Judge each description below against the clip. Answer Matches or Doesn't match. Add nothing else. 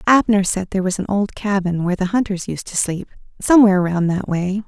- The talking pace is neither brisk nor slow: Doesn't match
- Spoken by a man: Doesn't match